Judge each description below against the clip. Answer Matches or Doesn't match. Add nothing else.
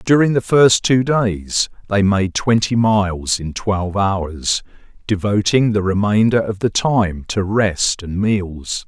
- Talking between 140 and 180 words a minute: Matches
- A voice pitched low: Matches